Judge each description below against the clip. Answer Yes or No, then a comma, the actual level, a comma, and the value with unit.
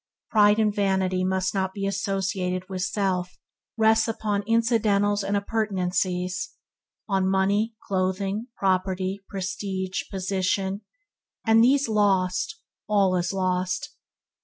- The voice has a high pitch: Yes, high, 195 Hz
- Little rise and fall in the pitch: Yes, narrow, 1.9 semitones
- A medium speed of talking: No, slow, 110 wpm